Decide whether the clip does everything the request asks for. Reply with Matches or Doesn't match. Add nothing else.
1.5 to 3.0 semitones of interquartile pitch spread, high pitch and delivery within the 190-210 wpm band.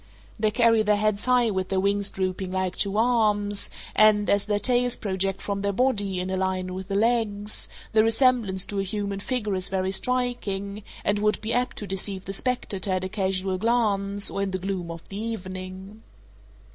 Matches